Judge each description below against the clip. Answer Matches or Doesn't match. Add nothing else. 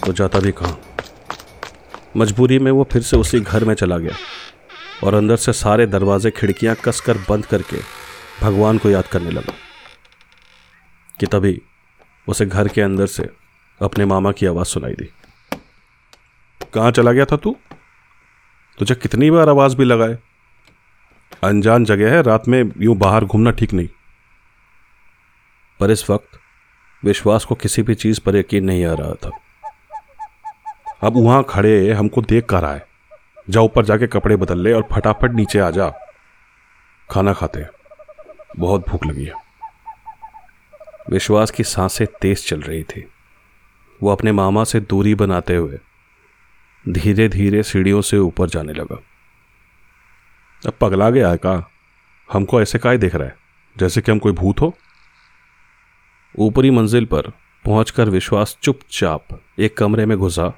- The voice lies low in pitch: Matches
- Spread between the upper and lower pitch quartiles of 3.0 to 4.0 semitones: Matches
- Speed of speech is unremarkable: Matches